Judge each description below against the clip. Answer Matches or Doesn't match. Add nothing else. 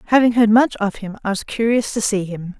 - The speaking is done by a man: Doesn't match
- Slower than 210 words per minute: Doesn't match